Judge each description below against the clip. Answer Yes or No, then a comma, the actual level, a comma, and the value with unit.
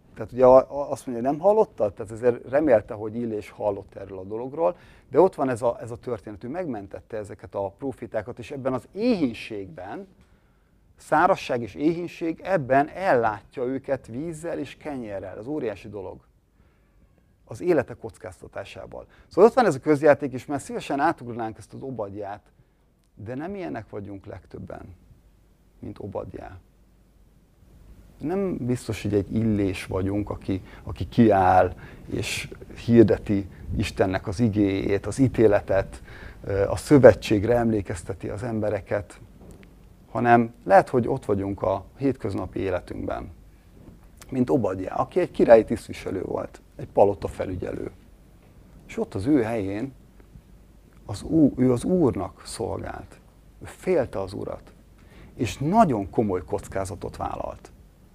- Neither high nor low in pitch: No, low, 115 Hz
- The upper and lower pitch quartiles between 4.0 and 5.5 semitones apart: Yes, average, 4.7 semitones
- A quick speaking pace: No, average, 130 wpm